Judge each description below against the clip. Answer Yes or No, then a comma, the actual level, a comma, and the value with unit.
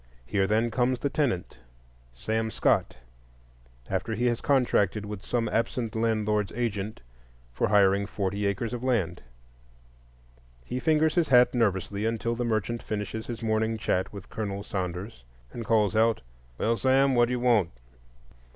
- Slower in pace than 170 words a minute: Yes, average, 150 wpm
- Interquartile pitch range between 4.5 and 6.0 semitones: No, average, 2.9 semitones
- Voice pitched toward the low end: Yes, low, 110 Hz